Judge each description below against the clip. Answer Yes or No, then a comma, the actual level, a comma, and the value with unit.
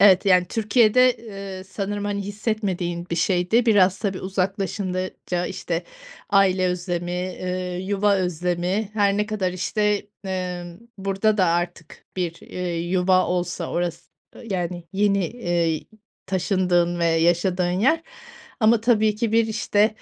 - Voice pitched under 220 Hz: Yes, medium, 185 Hz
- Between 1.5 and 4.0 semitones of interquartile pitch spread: Yes, narrow, 2.6 semitones